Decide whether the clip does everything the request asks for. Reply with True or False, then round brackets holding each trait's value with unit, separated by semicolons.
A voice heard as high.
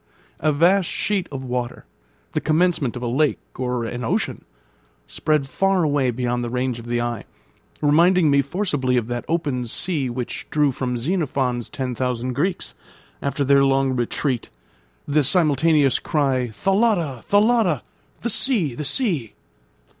False (140 Hz)